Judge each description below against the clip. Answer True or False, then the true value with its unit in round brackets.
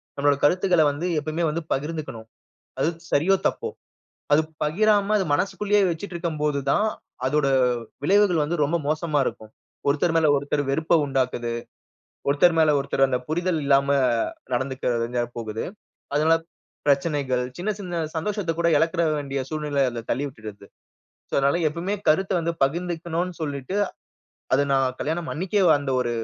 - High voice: False (155 Hz)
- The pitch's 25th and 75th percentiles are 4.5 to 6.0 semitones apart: False (3.8 semitones)